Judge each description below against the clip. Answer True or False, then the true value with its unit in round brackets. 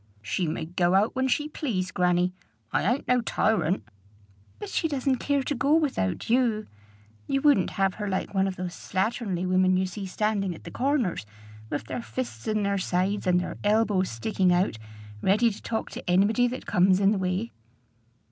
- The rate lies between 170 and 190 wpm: True (185 wpm)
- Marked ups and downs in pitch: False (4.5 semitones)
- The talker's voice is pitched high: True (195 Hz)